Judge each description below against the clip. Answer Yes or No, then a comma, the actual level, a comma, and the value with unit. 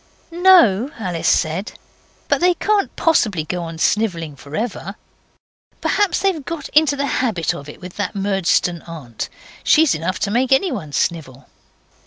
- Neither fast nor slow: Yes, average, 150 wpm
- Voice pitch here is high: Yes, high, 200 Hz